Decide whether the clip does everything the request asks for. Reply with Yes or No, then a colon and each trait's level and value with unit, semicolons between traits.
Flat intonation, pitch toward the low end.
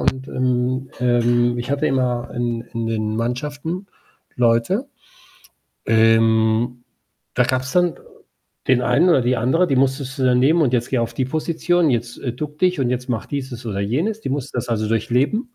No: average, 3.1 semitones; low, 125 Hz